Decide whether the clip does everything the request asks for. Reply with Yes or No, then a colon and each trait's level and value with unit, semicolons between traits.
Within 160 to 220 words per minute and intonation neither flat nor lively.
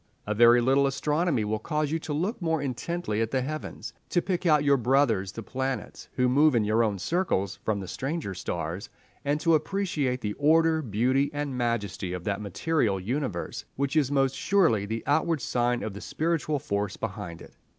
No: average, 190 wpm; wide, 6.3 semitones